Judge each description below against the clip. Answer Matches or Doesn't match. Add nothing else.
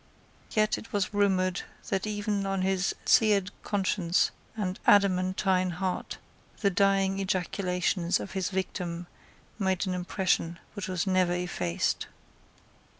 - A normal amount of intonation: Doesn't match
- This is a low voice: Doesn't match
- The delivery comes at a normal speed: Doesn't match